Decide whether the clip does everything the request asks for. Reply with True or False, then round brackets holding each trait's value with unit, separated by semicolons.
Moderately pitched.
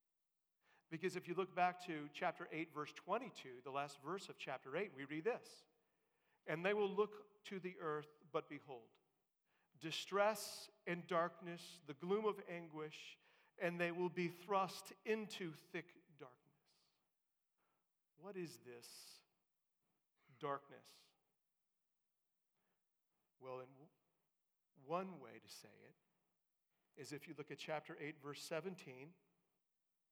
True (170 Hz)